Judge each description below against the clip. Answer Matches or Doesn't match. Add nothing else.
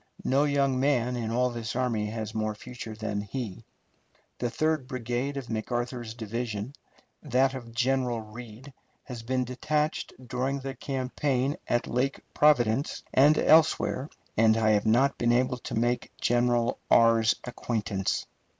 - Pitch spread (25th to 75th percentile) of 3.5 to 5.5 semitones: Doesn't match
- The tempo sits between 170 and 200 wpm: Doesn't match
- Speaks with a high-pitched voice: Doesn't match